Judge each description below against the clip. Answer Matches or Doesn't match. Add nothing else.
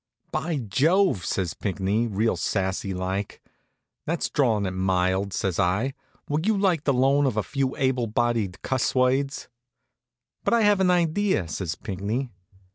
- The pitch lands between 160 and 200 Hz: Doesn't match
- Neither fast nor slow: Matches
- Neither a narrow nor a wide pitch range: Doesn't match